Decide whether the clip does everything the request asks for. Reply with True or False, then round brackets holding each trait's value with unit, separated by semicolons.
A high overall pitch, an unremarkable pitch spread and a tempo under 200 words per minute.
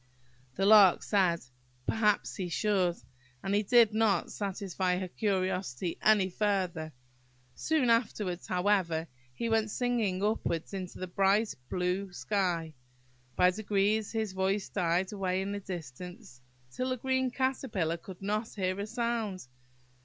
True (195 Hz; 3.1 semitones; 135 wpm)